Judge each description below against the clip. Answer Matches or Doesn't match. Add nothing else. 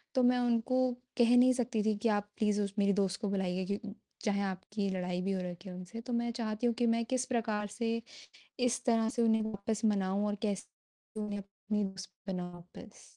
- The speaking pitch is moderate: Doesn't match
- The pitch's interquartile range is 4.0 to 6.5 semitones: Doesn't match